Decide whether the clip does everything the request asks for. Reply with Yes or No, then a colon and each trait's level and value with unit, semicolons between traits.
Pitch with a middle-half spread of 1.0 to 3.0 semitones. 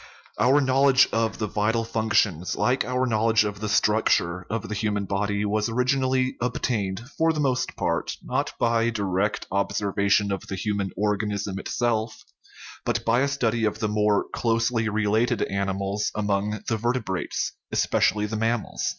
Yes: narrow, 2.5 semitones